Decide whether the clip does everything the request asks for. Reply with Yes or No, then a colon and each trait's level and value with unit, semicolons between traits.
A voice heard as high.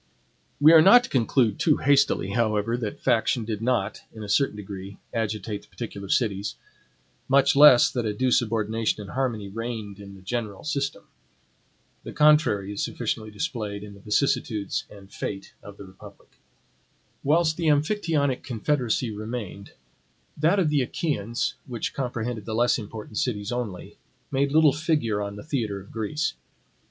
No: low, 115 Hz